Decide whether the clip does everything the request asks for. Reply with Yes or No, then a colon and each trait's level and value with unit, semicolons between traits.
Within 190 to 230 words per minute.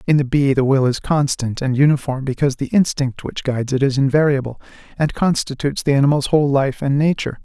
Yes: average, 200 wpm